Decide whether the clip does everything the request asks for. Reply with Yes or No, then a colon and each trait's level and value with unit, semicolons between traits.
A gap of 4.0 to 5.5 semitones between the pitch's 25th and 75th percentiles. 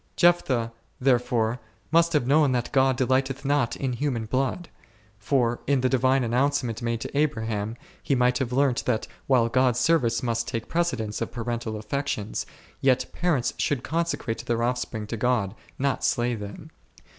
No: average, 2.9 semitones